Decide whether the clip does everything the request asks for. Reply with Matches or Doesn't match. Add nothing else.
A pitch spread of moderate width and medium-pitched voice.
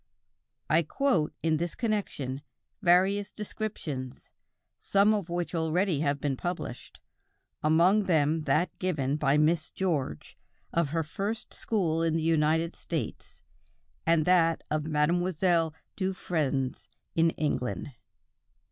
Matches